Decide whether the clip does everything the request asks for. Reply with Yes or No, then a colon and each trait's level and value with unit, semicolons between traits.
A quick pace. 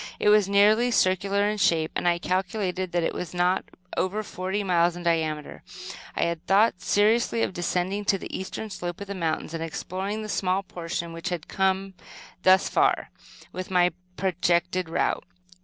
No: average, 175 wpm